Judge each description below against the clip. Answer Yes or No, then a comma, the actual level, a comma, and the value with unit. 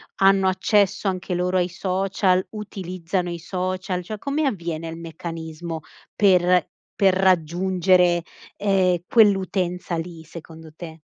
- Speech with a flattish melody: Yes, narrow, 2.1 semitones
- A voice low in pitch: No, medium, 180 Hz